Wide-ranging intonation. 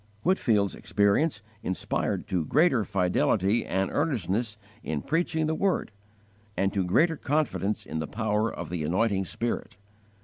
Yes: wide, 7.5 semitones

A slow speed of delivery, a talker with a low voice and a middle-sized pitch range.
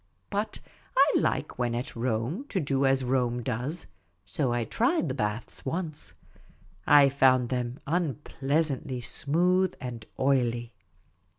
Yes: slow, 125 wpm; low, 130 Hz; average, 3.5 semitones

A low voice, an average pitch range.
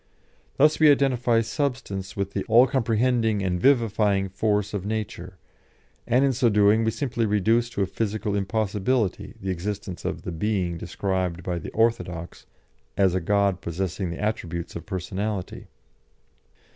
Yes: low, 105 Hz; average, 3.5 semitones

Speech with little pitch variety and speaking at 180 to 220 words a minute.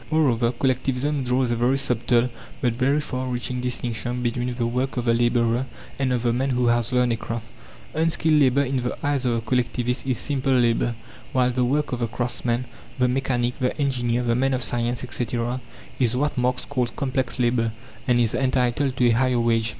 Yes: narrow, 1.6 semitones; average, 195 wpm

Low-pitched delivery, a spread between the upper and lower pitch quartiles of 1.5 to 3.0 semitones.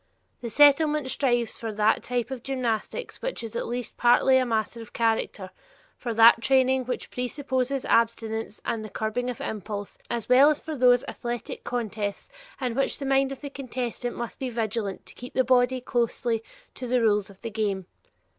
No: high, 240 Hz; narrow, 2.6 semitones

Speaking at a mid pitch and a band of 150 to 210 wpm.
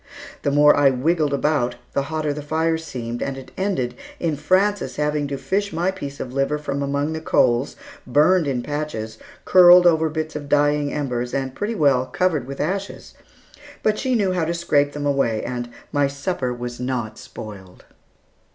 Yes: medium, 145 Hz; average, 180 wpm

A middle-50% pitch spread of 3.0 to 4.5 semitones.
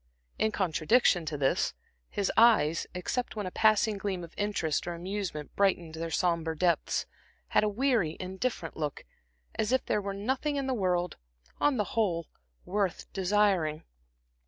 Yes: average, 4.2 semitones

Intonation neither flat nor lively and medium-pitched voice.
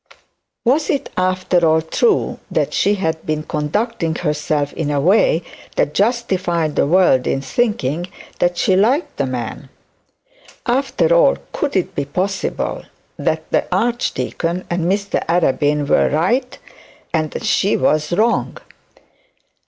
No: wide, 6.2 semitones; medium, 175 Hz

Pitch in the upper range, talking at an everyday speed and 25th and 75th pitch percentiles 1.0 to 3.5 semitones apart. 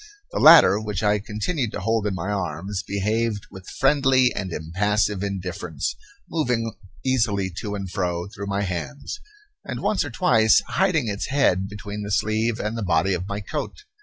No: low, 105 Hz; average, 170 wpm; average, 3.1 semitones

